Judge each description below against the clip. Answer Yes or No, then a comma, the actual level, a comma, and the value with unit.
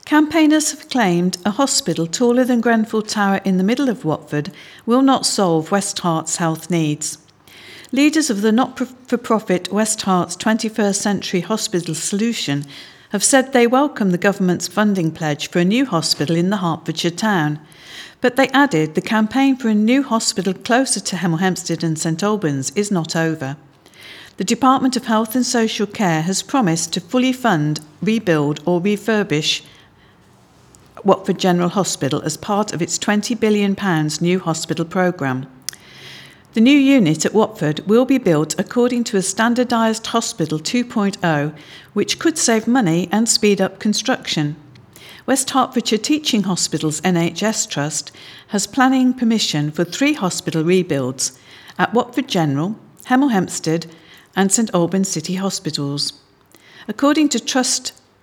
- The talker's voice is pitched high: Yes, high, 195 Hz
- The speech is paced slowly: No, average, 145 wpm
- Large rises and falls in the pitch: Yes, wide, 6.2 semitones